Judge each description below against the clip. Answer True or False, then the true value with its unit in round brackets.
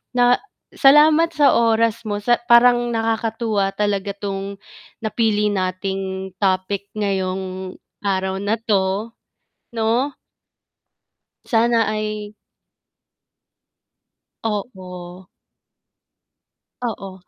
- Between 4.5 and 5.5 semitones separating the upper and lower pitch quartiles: False (3.1 semitones)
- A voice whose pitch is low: False (205 Hz)